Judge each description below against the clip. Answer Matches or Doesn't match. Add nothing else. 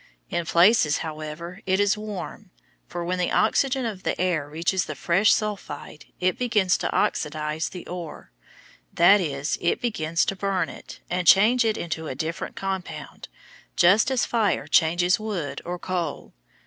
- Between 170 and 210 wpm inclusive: Doesn't match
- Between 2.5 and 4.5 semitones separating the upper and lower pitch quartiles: Matches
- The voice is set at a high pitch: Doesn't match